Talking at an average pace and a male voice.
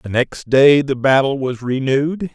Yes: average, 180 wpm; male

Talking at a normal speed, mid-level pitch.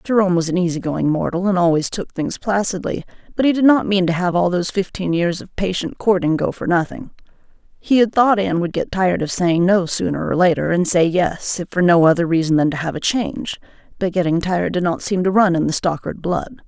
No: fast, 235 wpm; medium, 180 Hz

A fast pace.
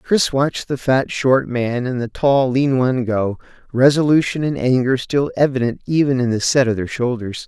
No: average, 195 wpm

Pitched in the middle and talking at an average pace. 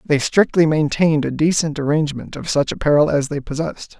Yes: medium, 150 Hz; average, 180 wpm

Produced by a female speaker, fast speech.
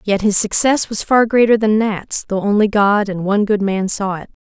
Yes: female; fast, 230 wpm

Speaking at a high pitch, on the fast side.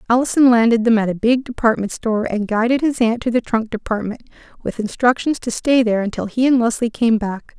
Yes: high, 230 Hz; fast, 215 wpm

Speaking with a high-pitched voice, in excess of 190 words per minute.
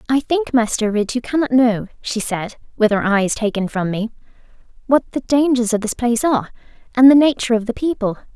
Yes: high, 235 Hz; average, 200 wpm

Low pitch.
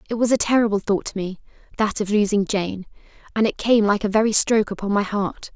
No: high, 210 Hz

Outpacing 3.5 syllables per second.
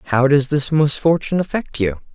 Yes: 5.0 syllables/s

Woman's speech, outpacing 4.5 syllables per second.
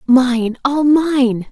No: female; 2.3 syllables/s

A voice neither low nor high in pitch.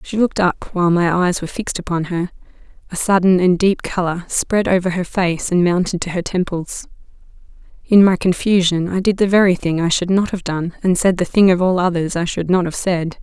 Yes: medium, 180 Hz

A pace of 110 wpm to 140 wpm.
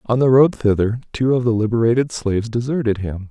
No: average, 200 wpm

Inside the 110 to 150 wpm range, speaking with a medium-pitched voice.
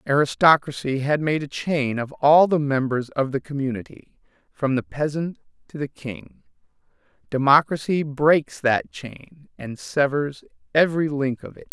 Yes: average, 145 wpm; medium, 145 Hz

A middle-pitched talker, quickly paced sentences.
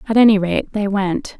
No: high, 205 Hz; fast, 215 wpm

